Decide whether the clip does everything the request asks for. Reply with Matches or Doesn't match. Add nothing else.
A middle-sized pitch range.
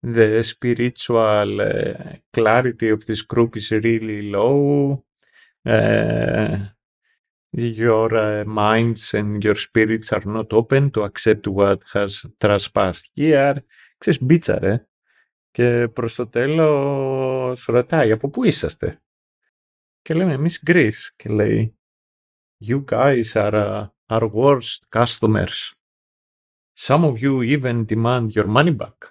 Matches